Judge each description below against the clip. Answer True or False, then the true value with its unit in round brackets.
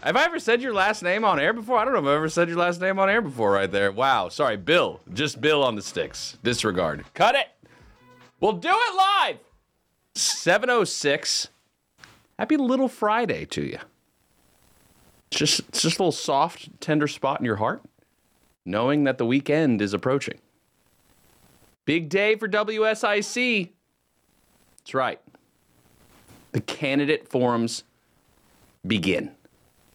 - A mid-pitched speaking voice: True (155 Hz)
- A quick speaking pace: False (145 wpm)